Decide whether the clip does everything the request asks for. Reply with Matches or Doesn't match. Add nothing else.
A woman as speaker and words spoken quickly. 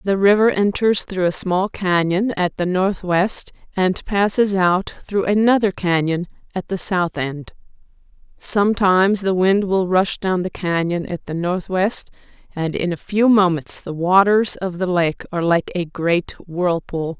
Doesn't match